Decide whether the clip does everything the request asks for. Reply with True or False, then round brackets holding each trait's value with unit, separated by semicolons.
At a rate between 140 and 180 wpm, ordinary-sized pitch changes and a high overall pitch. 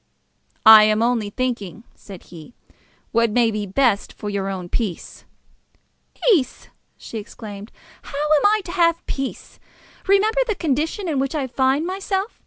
False (155 wpm; 7.6 semitones; 255 Hz)